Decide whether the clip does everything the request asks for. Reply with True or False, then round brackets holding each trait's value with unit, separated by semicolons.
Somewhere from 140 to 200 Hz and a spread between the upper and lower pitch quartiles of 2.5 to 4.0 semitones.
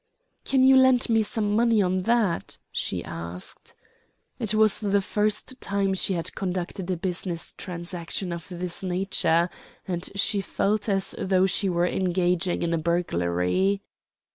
True (190 Hz; 3.0 semitones)